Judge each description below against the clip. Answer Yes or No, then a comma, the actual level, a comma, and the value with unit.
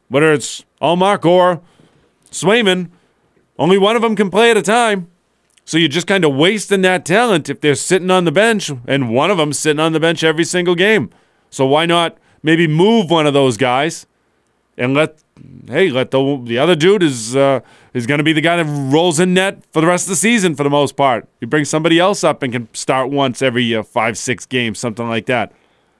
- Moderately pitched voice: Yes, medium, 160 Hz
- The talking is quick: Yes, fast, 220 wpm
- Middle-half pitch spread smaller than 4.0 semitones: No, average, 5.1 semitones